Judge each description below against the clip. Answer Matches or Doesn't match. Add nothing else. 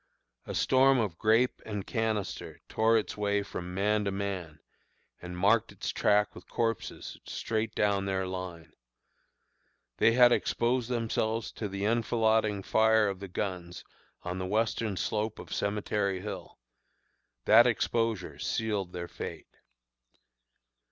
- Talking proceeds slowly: Matches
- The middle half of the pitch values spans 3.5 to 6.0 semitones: Doesn't match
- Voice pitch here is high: Doesn't match